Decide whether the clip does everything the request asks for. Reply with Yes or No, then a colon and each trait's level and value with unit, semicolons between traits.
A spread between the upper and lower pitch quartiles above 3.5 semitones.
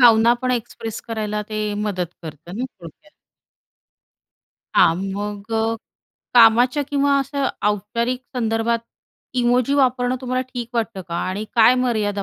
No: average, 3.1 semitones